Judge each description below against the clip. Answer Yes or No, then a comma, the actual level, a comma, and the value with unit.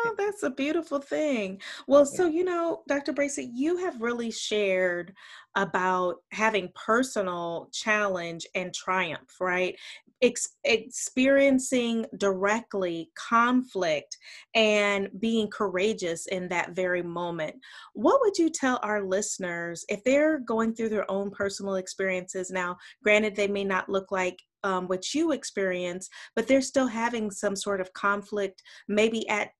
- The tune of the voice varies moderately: Yes, average, 4.8 semitones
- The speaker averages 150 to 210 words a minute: No, slow, 135 wpm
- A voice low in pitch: No, high, 205 Hz